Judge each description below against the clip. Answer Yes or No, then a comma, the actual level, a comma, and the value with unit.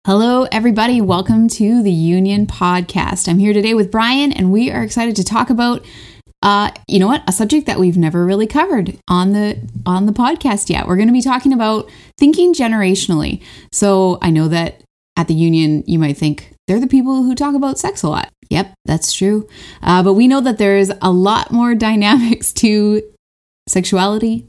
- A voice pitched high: Yes, high, 210 Hz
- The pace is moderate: Yes, average, 190 wpm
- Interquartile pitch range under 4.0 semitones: No, average, 4.5 semitones